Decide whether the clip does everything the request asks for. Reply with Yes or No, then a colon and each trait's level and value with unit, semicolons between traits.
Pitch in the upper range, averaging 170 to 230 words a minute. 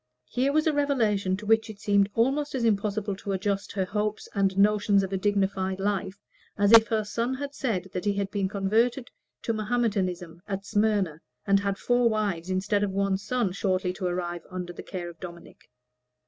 Yes: high, 200 Hz; average, 190 wpm